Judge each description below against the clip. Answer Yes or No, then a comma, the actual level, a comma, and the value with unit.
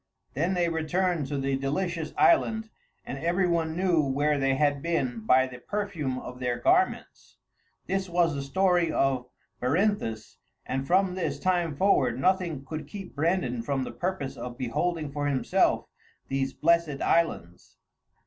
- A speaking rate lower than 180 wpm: Yes, average, 150 wpm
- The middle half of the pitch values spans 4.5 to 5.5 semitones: Yes, average, 5.0 semitones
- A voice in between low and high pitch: Yes, medium, 155 Hz